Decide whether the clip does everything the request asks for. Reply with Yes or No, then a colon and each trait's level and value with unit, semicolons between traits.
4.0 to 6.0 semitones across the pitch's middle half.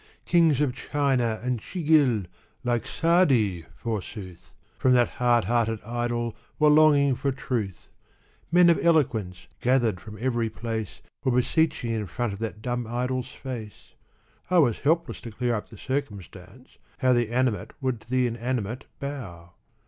No: average, 3.4 semitones